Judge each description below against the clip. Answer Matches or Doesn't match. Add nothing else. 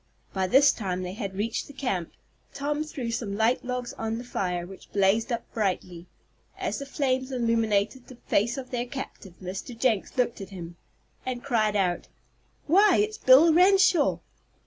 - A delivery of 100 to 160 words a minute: Doesn't match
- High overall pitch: Matches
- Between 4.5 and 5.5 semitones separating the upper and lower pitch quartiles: Matches